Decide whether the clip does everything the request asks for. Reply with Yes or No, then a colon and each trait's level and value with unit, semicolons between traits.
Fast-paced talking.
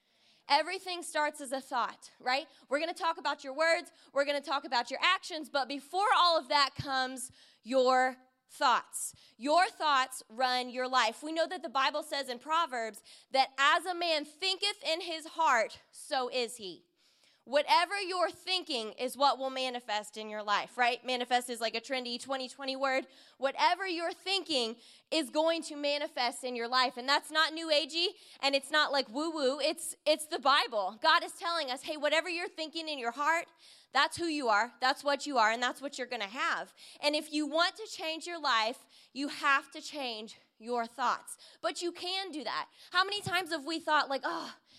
No: average, 195 wpm